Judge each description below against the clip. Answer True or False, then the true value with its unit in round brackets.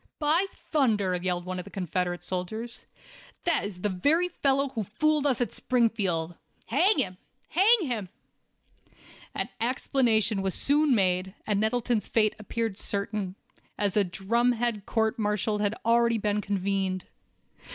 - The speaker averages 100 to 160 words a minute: True (140 wpm)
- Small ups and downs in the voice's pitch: False (4.4 semitones)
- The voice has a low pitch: False (215 Hz)